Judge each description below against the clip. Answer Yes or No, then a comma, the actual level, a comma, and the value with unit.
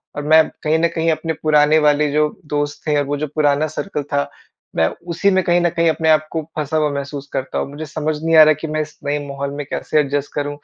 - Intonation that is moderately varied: No, narrow, 1.6 semitones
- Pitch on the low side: No, medium, 150 Hz